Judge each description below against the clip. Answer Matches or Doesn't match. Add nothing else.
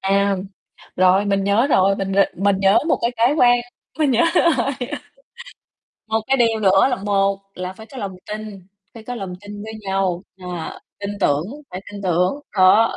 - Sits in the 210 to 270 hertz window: Doesn't match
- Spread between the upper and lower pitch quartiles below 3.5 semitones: Matches